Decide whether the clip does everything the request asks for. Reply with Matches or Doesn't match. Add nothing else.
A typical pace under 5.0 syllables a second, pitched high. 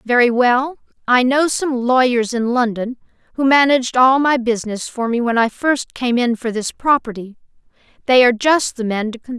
Doesn't match